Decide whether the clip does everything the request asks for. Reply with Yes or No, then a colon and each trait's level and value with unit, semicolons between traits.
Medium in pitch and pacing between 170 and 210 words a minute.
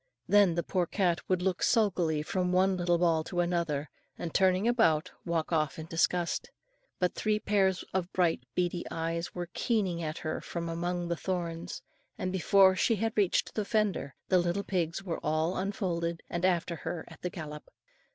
Yes: medium, 175 Hz; average, 180 wpm